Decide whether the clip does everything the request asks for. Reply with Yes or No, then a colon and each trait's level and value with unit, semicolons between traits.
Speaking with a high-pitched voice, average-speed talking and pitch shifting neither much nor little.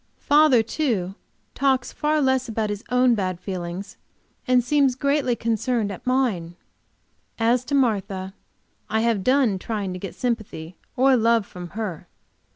Yes: high, 230 Hz; average, 145 wpm; average, 4.9 semitones